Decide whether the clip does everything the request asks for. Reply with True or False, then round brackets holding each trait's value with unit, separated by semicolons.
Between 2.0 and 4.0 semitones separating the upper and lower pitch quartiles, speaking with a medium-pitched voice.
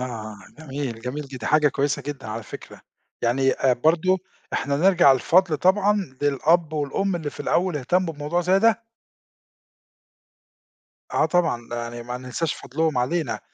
False (5.4 semitones; 145 Hz)